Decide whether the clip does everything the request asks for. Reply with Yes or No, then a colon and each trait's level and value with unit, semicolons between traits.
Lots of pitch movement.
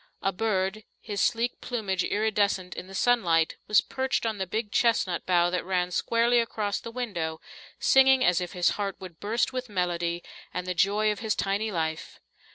No: average, 3.9 semitones